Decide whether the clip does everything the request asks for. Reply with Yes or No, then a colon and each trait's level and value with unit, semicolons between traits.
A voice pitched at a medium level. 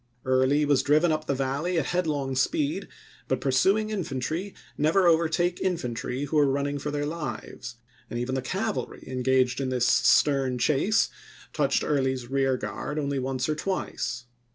Yes: medium, 145 Hz